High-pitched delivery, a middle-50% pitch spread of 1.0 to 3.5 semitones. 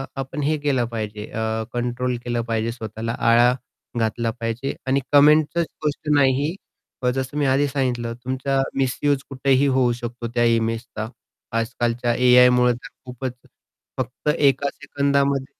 No: low, 125 Hz; average, 2.9 semitones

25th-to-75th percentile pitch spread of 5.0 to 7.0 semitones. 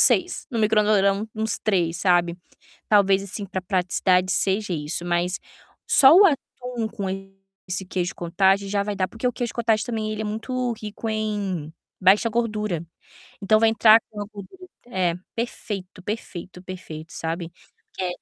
No: average, 3.3 semitones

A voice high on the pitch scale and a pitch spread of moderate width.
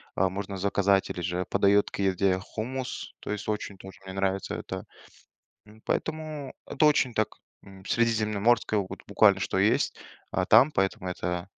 No: low, 100 Hz; average, 3.0 semitones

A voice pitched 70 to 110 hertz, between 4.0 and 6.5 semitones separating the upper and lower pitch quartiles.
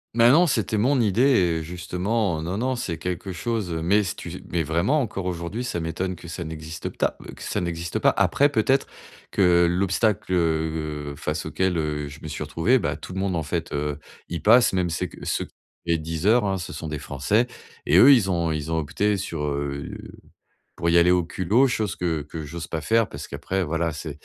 Yes: very low, 85 Hz; average, 4.4 semitones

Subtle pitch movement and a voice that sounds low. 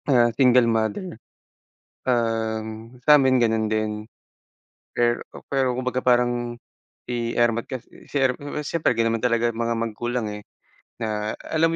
Yes: narrow, 2.1 semitones; low, 120 Hz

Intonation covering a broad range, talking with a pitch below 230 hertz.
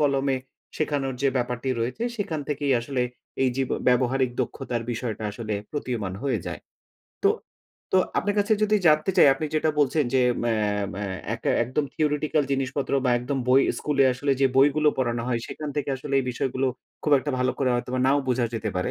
No: average, 3.0 semitones; low, 135 Hz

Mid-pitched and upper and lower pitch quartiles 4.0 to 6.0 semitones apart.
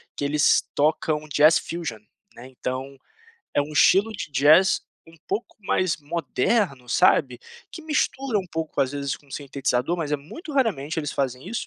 Yes: medium, 150 Hz; average, 5.0 semitones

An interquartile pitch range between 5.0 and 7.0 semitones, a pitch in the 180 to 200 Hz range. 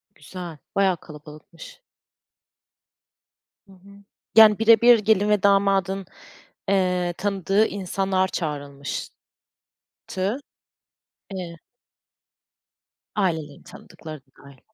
No: average, 3.7 semitones; high, 190 Hz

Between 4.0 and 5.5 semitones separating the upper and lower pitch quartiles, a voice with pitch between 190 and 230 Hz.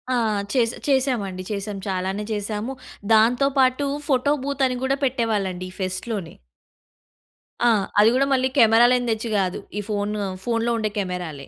Yes: average, 4.3 semitones; high, 225 Hz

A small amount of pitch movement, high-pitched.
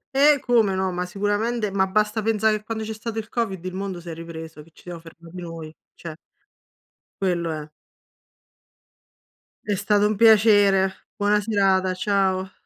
No: average, 3.1 semitones; high, 195 Hz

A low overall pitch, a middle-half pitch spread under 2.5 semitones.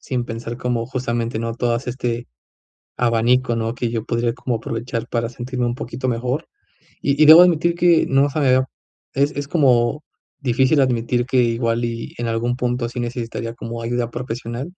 Yes: low, 120 Hz; narrow, 1.9 semitones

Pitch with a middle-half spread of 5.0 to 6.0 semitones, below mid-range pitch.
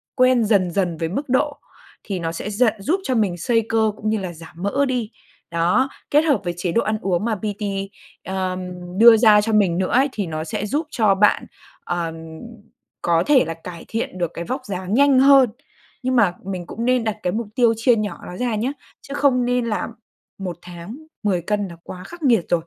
No: wide, 5.4 semitones; high, 210 Hz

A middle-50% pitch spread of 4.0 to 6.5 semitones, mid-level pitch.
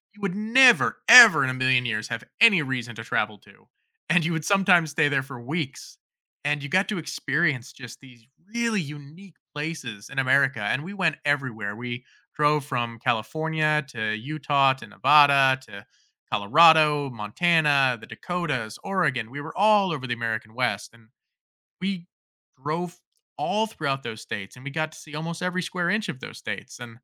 Yes: wide, 5.5 semitones; medium, 145 Hz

